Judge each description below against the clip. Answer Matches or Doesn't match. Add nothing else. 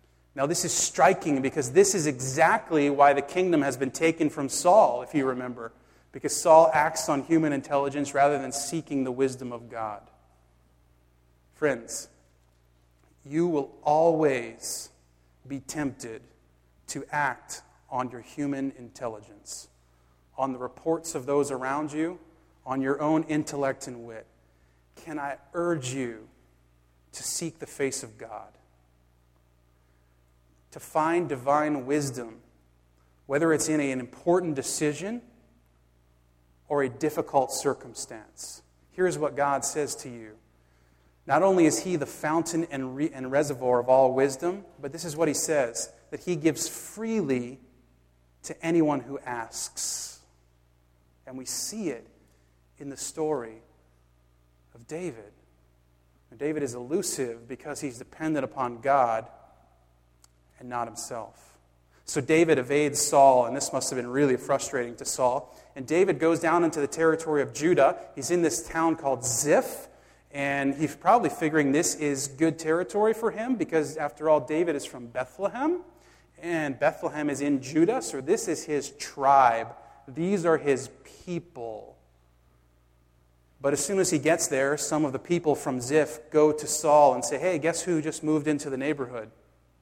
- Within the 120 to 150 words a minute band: Matches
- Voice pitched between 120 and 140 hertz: Matches